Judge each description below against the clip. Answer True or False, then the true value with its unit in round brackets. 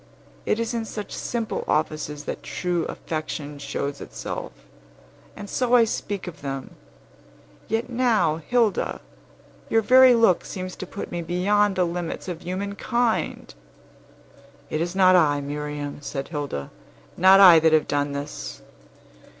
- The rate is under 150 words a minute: True (140 wpm)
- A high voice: False (180 Hz)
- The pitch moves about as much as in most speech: False (5.9 semitones)